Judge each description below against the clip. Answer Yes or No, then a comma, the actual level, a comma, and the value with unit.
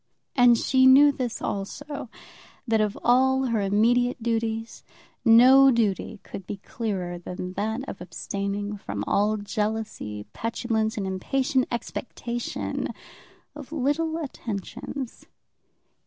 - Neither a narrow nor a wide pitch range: Yes, average, 4.2 semitones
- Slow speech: Yes, slow, 110 wpm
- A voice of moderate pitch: No, high, 225 Hz